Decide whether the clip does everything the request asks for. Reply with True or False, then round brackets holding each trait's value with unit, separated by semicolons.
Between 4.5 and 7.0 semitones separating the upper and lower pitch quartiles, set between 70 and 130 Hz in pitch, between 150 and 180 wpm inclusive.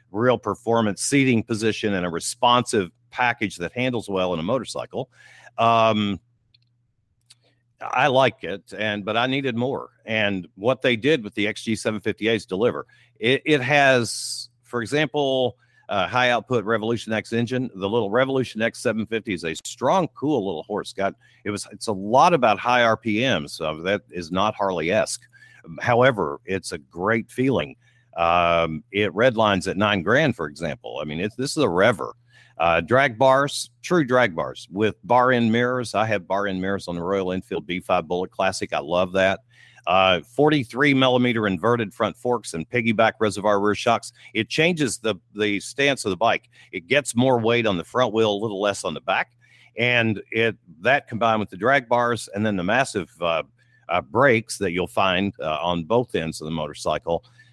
False (3.5 semitones; 115 Hz; 175 wpm)